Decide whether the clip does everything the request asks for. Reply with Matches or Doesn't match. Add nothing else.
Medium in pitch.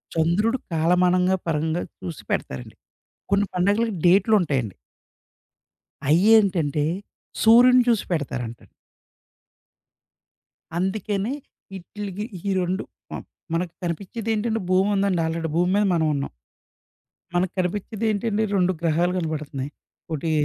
Matches